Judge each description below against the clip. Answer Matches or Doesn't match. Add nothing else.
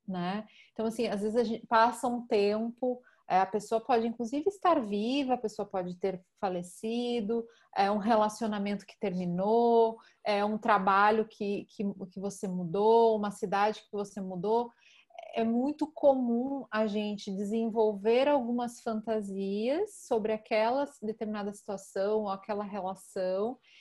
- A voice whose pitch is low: Doesn't match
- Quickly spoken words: Doesn't match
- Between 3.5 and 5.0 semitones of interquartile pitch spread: Doesn't match